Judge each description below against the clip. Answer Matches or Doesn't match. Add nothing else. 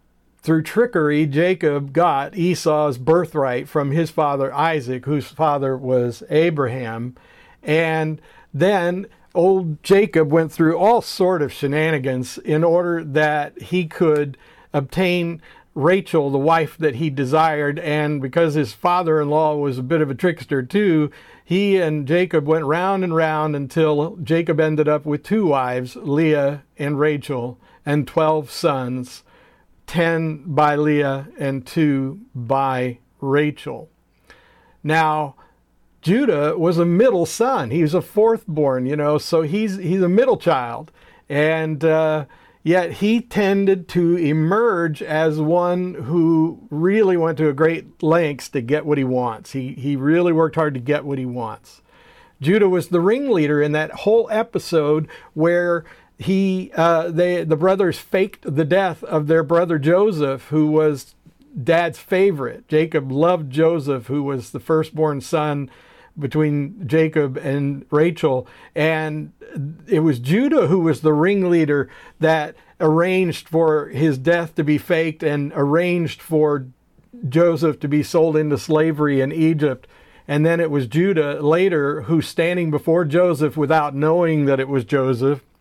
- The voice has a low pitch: Doesn't match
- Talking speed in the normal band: Matches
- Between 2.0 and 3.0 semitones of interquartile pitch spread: Matches